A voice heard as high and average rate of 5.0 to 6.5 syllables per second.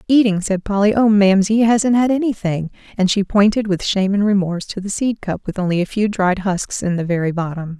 Yes: high, 200 Hz; 5.7 syllables/s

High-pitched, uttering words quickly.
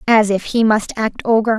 Yes: high, 220 Hz; fast, 230 wpm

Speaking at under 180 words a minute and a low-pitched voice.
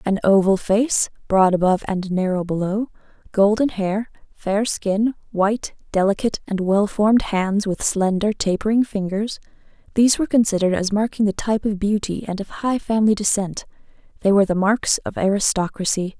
No: average, 155 wpm; high, 205 Hz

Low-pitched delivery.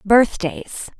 No: high, 210 Hz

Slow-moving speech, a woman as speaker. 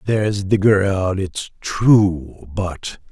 No: slow, 115 wpm; male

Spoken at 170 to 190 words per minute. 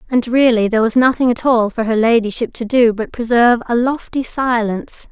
No: average, 200 wpm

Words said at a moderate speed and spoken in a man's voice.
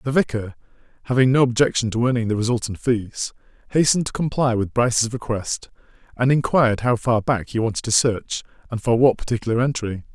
Yes: average, 175 wpm; male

